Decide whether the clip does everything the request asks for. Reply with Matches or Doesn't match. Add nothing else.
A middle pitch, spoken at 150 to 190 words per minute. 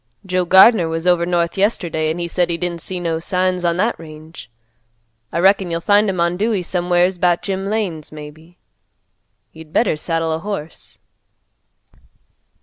Matches